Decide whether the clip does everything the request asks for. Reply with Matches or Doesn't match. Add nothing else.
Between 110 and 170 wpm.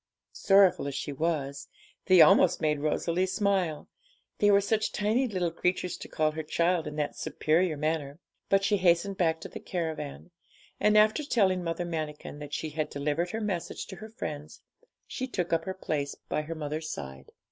Doesn't match